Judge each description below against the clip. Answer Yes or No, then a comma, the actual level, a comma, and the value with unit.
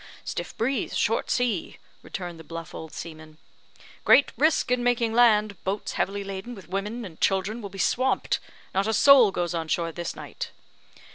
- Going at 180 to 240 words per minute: No, average, 170 wpm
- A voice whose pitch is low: No, high, 200 Hz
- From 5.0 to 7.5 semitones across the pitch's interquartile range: Yes, average, 5.3 semitones